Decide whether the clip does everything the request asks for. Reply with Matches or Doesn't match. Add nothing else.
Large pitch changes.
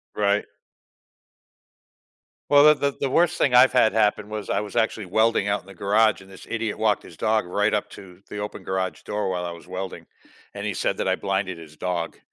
Doesn't match